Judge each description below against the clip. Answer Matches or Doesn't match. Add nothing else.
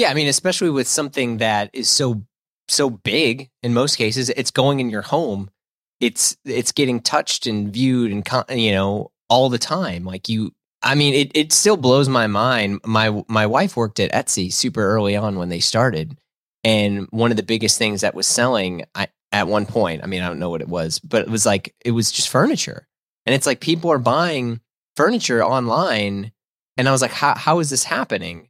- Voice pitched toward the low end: Matches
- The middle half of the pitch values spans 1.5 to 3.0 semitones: Doesn't match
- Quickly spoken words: Matches